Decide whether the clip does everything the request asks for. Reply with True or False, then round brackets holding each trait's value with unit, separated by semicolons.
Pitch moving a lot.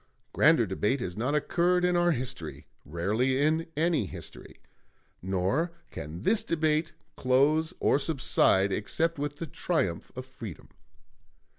True (7.5 semitones)